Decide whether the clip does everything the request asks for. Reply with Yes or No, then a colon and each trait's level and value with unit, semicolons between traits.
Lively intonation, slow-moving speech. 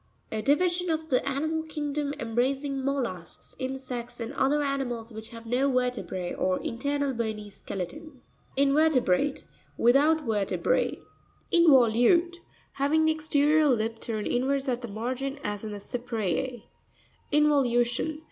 No: average, 4.1 semitones; slow, 125 wpm